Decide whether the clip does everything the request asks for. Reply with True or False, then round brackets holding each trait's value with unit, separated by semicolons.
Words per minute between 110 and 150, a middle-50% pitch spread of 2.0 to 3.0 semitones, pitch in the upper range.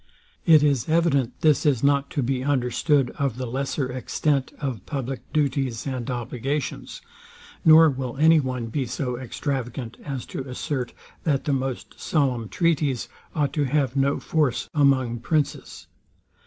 False (145 wpm; 2.5 semitones; 135 Hz)